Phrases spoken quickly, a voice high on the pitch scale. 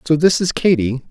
No: fast, 215 wpm; medium, 155 Hz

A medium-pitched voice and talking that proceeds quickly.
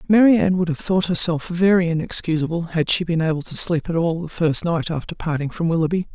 Yes: medium, 170 Hz; fast, 215 wpm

